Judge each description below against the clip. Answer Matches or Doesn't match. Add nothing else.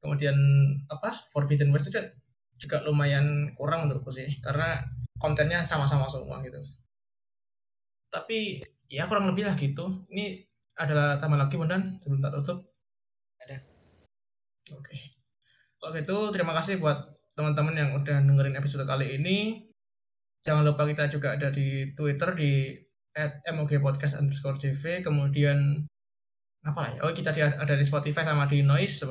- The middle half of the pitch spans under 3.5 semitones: Matches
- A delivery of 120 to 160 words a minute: Matches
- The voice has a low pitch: Doesn't match